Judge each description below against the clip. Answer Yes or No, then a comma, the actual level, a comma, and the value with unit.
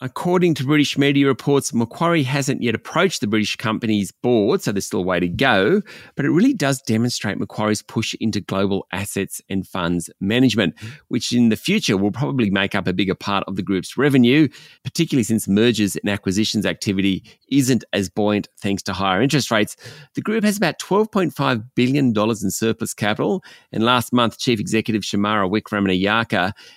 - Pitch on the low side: Yes, low, 115 Hz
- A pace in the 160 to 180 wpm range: Yes, average, 175 wpm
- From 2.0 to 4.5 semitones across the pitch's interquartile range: No, wide, 5.4 semitones